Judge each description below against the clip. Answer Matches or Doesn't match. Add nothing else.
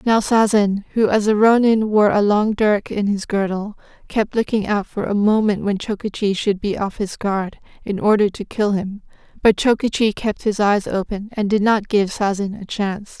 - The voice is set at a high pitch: Matches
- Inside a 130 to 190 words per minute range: Doesn't match